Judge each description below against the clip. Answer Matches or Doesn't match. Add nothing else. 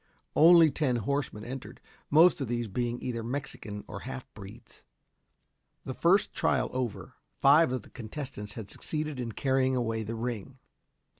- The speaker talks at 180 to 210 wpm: Doesn't match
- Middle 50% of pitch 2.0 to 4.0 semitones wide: Matches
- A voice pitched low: Matches